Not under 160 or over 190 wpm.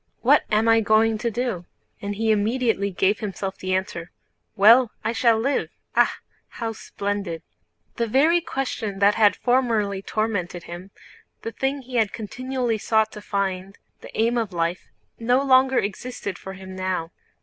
No: average, 150 wpm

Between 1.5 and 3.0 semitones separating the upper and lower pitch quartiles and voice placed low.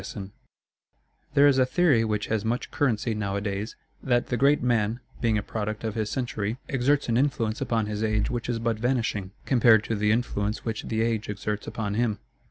Yes: narrow, 2.5 semitones; low, 115 Hz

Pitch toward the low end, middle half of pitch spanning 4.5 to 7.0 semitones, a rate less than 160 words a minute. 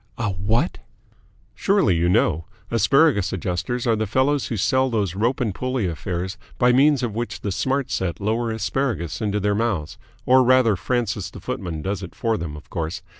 No: low, 110 Hz; average, 5.2 semitones; average, 180 wpm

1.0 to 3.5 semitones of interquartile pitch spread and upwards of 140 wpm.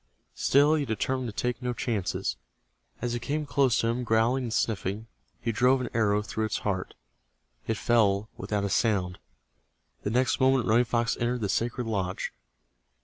Yes: average, 2.9 semitones; average, 170 wpm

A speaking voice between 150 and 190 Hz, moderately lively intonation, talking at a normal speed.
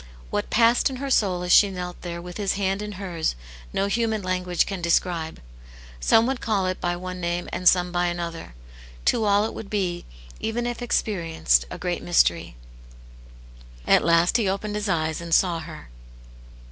Yes: medium, 185 Hz; average, 3.3 semitones; average, 180 wpm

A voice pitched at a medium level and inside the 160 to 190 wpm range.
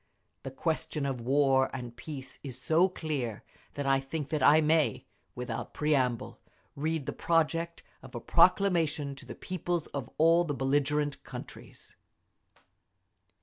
No: medium, 145 Hz; average, 140 wpm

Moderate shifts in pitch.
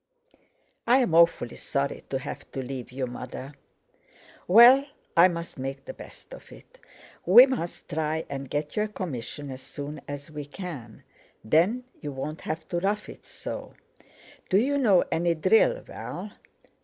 No: wide, 7.2 semitones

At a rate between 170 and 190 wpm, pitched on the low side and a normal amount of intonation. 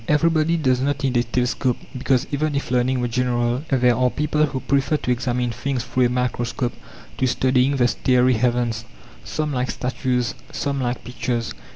No: average, 175 wpm; low, 125 Hz; narrow, 1.9 semitones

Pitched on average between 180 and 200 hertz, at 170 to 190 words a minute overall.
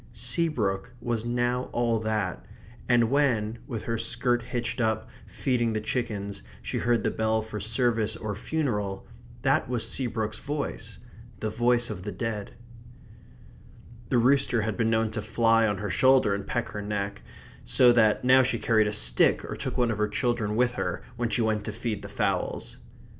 No: low, 115 Hz; average, 175 wpm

